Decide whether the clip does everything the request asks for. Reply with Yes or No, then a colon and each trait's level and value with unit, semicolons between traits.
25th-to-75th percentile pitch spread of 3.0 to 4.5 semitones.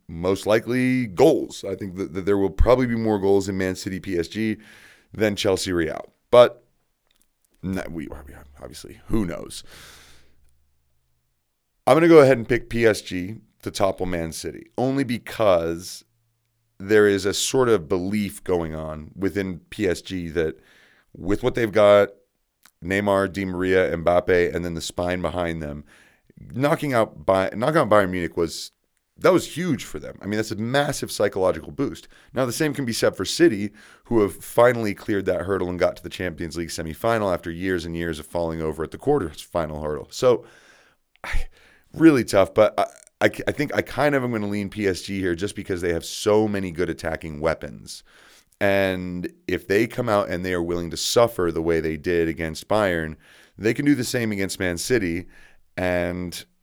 Yes: average, 4.2 semitones